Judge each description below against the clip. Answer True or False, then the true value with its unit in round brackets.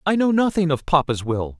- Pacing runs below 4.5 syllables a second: False (5.4 syllables/s)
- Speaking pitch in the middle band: True (160 Hz)